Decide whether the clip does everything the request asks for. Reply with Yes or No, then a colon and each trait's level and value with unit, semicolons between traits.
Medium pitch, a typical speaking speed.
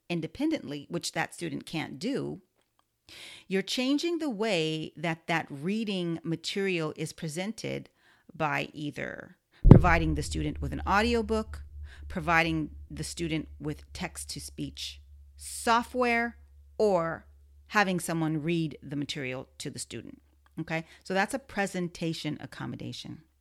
No: medium, 160 Hz; slow, 120 wpm